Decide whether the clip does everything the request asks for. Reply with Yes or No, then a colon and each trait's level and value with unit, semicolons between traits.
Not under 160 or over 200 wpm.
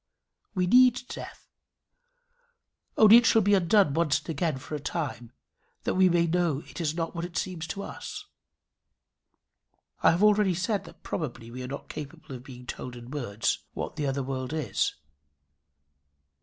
Yes: average, 170 wpm